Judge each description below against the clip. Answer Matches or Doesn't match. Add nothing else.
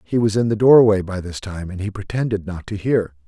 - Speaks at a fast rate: Matches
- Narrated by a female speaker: Doesn't match